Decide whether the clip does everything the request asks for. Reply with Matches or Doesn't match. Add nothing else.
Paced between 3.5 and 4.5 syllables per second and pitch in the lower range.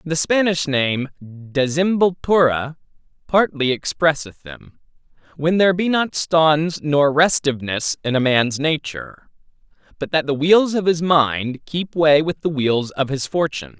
Doesn't match